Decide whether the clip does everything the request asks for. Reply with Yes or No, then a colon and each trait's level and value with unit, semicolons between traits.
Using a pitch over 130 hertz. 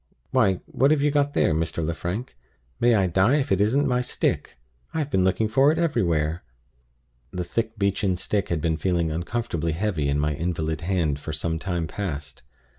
No: very low, 95 Hz